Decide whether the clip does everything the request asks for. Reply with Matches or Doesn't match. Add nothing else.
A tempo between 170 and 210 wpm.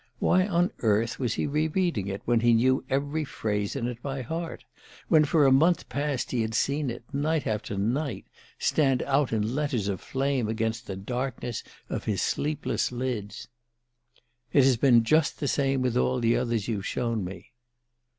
Matches